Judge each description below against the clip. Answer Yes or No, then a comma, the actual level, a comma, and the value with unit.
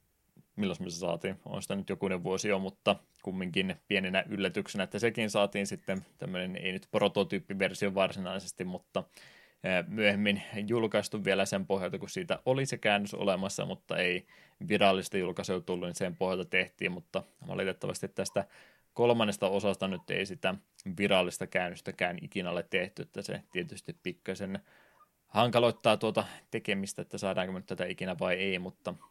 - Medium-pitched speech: No, low, 100 Hz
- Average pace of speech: Yes, average, 145 wpm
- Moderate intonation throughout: No, narrow, 1.8 semitones